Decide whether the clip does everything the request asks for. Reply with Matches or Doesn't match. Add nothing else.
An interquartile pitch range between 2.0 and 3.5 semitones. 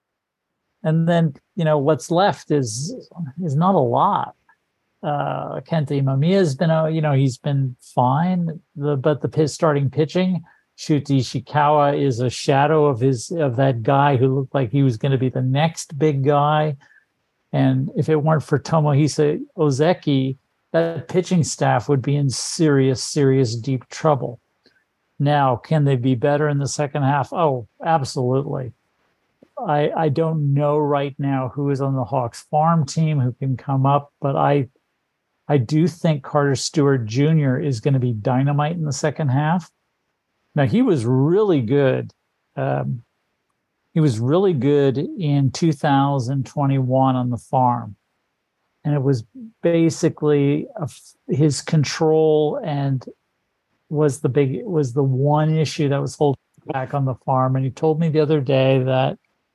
Matches